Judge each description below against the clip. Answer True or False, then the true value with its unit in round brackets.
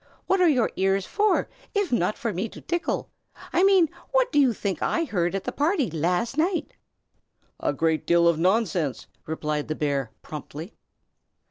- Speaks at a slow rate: False (170 wpm)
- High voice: True (195 Hz)